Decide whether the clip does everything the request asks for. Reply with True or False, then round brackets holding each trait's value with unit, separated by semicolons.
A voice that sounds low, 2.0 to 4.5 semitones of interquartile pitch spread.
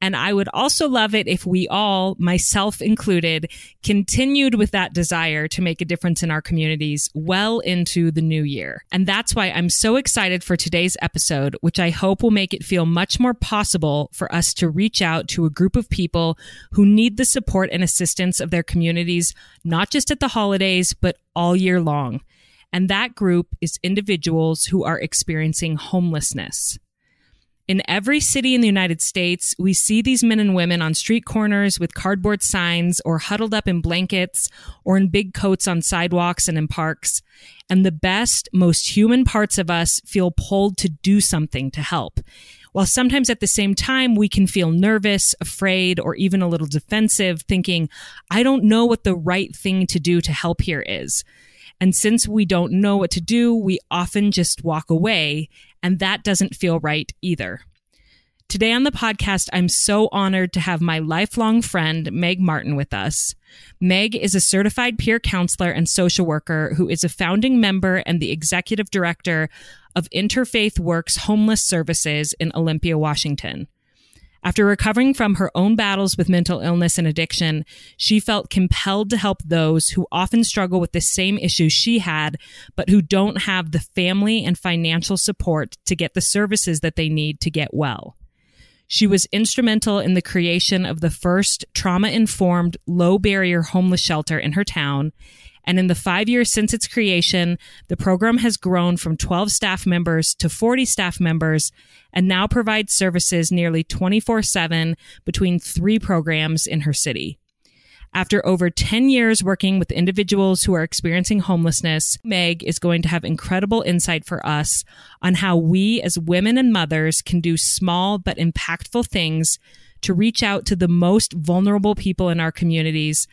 False (180 Hz; 3.4 semitones)